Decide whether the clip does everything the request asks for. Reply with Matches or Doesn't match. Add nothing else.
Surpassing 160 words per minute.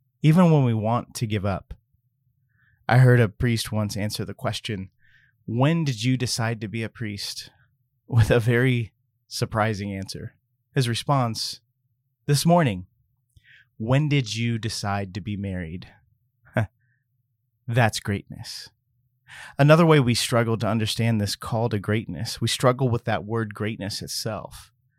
Doesn't match